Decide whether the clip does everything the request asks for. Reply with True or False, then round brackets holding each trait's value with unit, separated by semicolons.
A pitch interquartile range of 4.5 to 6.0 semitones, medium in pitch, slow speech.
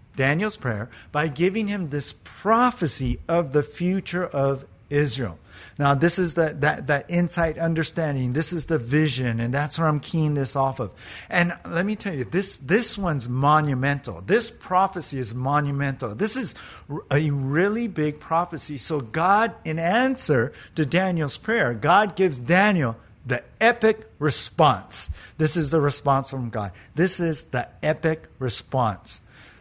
False (5.0 semitones; 150 Hz; 150 wpm)